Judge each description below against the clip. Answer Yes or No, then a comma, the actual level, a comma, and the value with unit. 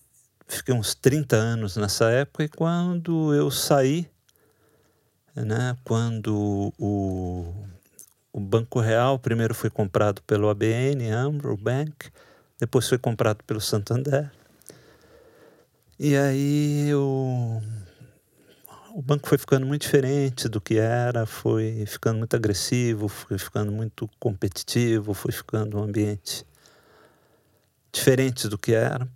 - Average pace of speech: No, slow, 115 wpm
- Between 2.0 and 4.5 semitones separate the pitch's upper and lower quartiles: Yes, average, 4.1 semitones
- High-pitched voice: No, low, 115 Hz